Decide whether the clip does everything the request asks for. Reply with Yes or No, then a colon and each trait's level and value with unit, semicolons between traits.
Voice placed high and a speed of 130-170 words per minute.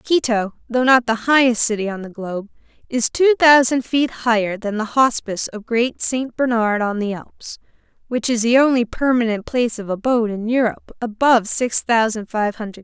No: high, 230 Hz; average, 185 wpm